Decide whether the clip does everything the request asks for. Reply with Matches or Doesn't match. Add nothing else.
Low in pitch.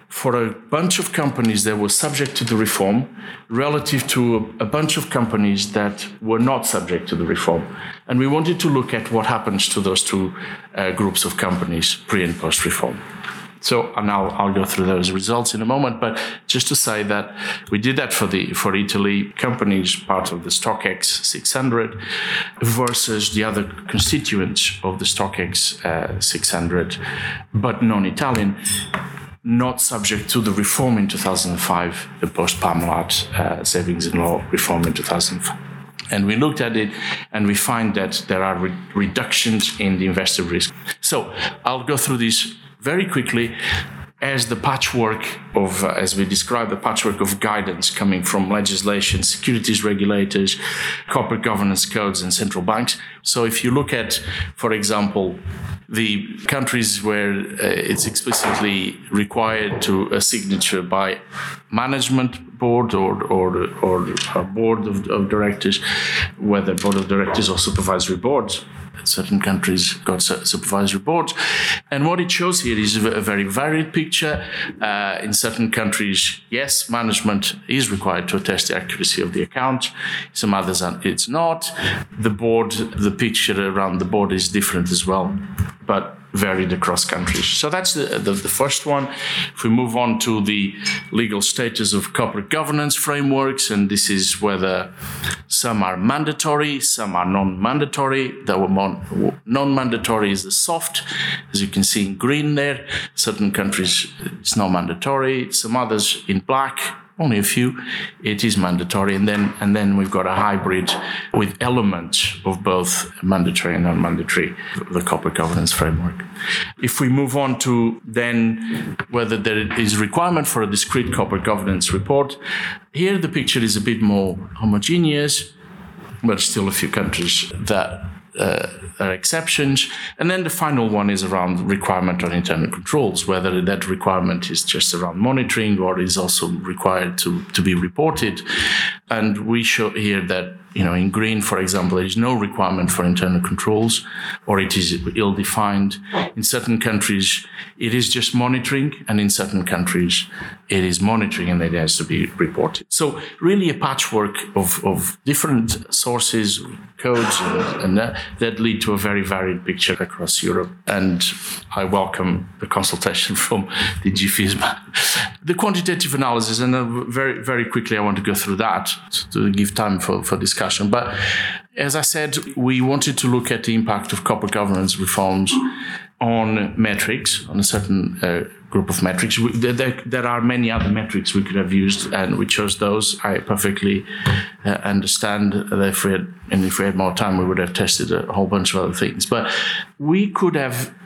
Matches